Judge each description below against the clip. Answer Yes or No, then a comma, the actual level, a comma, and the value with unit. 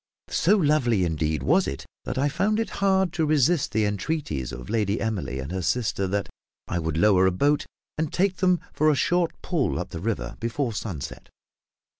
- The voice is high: No, low, 115 Hz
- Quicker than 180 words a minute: Yes, average, 190 wpm